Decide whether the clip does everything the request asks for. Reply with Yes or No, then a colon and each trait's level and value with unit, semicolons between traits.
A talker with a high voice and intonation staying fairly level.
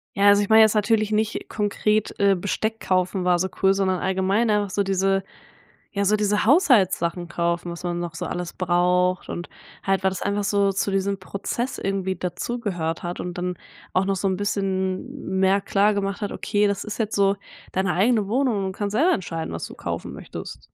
Yes: high, 195 Hz; narrow, 2.0 semitones